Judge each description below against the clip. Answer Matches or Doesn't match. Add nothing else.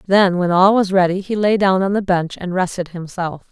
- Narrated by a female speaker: Matches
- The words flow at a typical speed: Doesn't match